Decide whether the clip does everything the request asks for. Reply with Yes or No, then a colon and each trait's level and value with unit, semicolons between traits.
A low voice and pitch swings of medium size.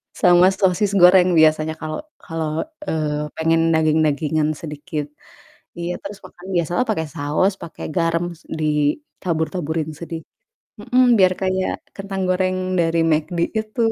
No: medium, 170 Hz; average, 3.0 semitones